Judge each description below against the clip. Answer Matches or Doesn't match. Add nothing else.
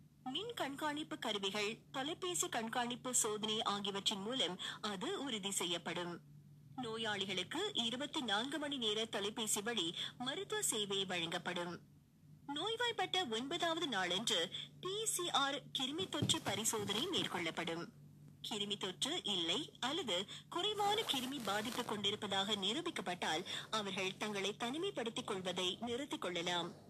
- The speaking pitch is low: Doesn't match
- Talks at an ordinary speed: Matches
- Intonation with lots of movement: Matches